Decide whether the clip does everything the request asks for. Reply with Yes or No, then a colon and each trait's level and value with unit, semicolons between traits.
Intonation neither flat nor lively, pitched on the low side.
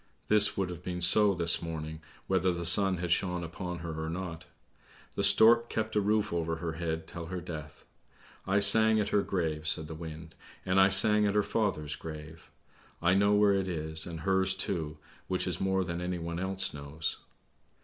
Yes: average, 3.3 semitones; very low, 90 Hz